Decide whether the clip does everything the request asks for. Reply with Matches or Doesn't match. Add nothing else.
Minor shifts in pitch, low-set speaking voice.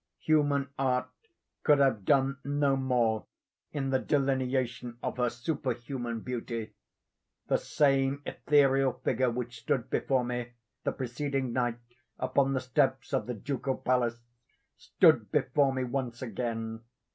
Matches